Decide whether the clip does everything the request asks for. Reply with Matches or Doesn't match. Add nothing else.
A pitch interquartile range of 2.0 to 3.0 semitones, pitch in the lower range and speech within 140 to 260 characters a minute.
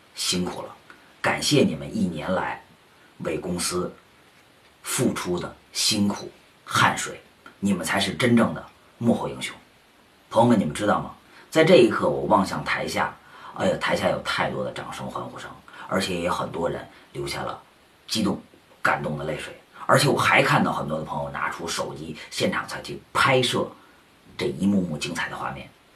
Matches